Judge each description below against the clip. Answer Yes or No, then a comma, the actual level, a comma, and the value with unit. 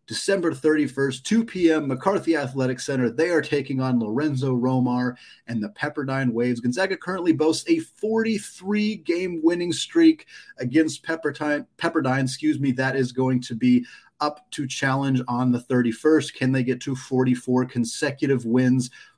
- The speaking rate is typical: Yes, average, 155 wpm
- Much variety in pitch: No, average, 4.3 semitones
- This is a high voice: No, medium, 140 Hz